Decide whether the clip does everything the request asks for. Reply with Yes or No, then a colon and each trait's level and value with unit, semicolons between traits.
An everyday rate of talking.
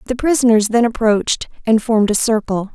Yes: average, 175 wpm